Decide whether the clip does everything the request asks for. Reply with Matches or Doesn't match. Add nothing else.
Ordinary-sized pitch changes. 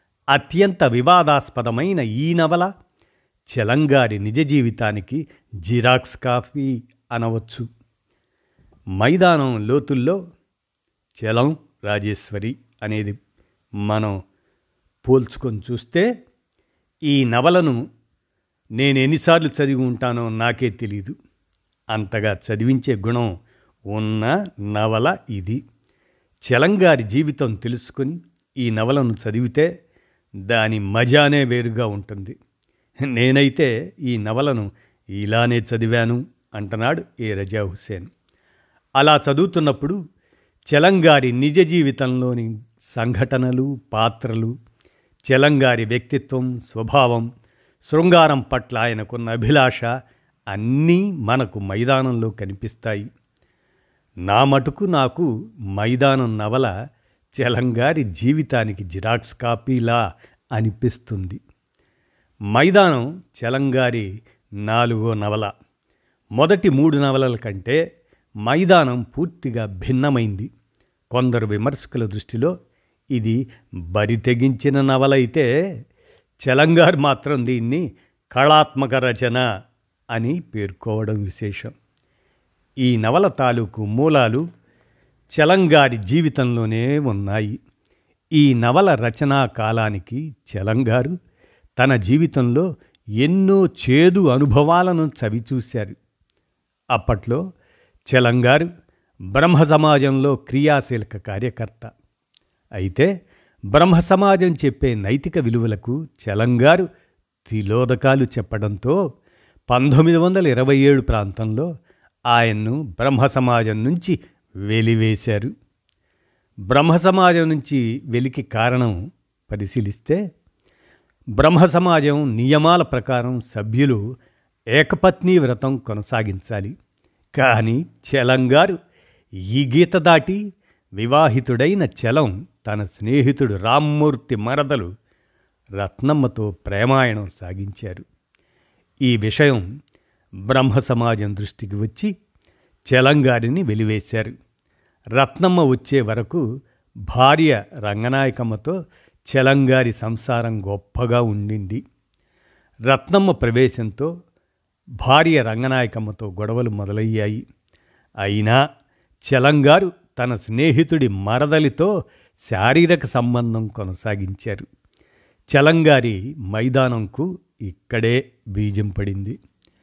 Matches